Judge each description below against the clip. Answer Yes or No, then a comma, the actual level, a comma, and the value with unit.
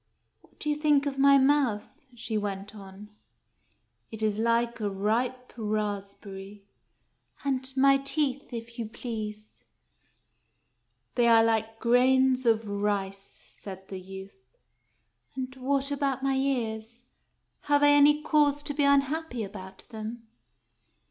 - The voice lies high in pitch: Yes, high, 235 Hz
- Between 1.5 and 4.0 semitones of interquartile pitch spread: No, average, 4.6 semitones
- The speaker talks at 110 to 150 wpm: Yes, average, 145 wpm